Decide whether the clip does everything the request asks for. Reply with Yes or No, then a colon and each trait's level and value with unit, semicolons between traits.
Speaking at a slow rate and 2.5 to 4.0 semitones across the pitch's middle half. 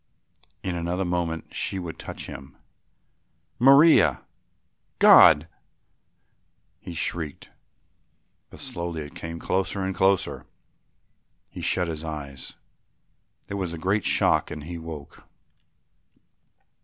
Yes: slow, 105 wpm; average, 3.0 semitones